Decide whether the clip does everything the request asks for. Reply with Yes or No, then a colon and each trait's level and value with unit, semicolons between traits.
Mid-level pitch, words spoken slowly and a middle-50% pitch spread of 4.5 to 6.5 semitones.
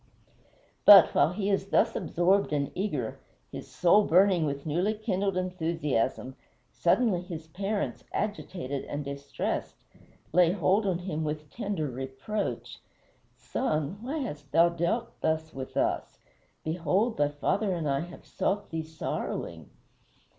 Yes: medium, 170 Hz; slow, 130 wpm; average, 4.9 semitones